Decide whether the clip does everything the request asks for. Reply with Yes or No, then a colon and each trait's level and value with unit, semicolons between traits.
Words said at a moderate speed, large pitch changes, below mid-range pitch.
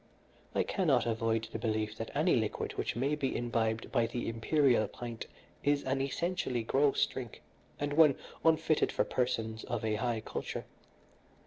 No: average, 155 wpm; average, 4.1 semitones; low, 120 Hz